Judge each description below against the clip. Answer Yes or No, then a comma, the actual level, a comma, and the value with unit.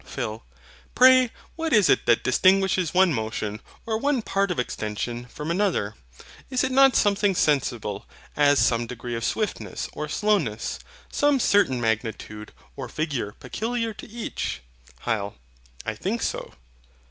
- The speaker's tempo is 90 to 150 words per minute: Yes, average, 140 wpm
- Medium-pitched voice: Yes, medium, 155 Hz